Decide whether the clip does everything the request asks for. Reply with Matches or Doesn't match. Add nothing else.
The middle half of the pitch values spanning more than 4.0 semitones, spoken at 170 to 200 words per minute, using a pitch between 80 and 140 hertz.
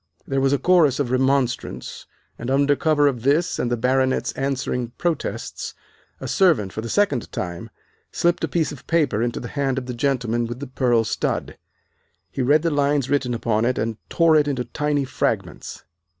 Doesn't match